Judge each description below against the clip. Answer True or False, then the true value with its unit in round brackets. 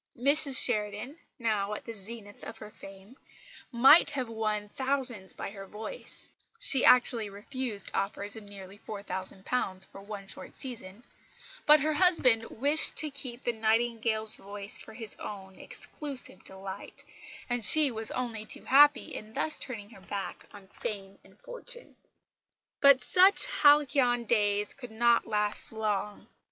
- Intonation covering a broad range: False (4.2 semitones)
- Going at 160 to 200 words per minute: False (145 wpm)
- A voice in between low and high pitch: False (225 Hz)